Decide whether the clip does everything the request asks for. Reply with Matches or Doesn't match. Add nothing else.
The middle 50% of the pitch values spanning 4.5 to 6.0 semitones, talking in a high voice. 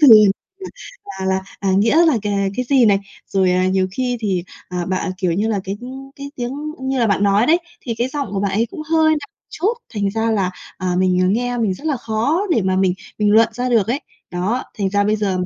Matches